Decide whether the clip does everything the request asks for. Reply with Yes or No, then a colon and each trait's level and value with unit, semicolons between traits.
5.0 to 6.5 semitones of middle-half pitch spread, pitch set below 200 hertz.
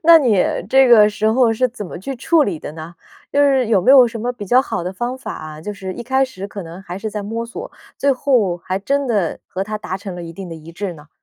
No: wide, 5.5 semitones; high, 210 Hz